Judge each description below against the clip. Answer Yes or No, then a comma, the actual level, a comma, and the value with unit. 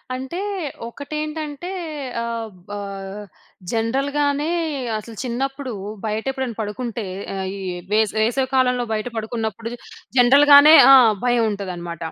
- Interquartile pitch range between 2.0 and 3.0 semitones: No, average, 4.1 semitones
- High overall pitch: Yes, high, 240 Hz